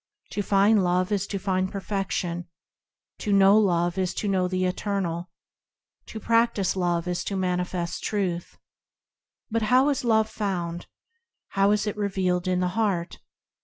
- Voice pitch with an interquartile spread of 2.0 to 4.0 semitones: Yes, narrow, 2.5 semitones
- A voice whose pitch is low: No, high, 190 Hz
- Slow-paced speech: No, average, 150 wpm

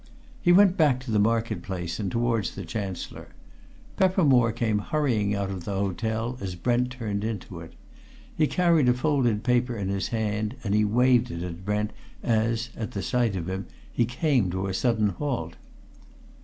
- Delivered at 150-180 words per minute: Yes, average, 175 wpm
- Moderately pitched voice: No, low, 110 Hz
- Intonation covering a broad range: No, average, 4.0 semitones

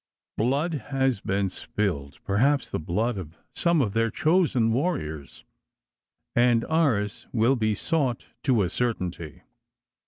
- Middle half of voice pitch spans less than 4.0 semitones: No, wide, 5.6 semitones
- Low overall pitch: Yes, low, 115 Hz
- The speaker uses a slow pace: Yes, slow, 125 wpm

